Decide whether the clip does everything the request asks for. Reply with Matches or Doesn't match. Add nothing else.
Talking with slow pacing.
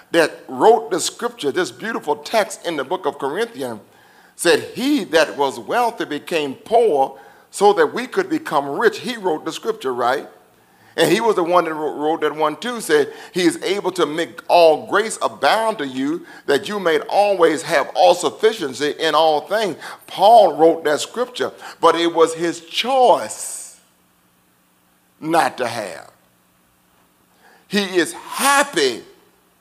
Doesn't match